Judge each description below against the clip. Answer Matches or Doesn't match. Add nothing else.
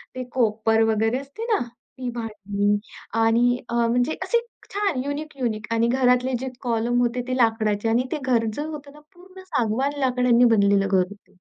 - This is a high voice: Matches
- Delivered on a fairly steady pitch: Doesn't match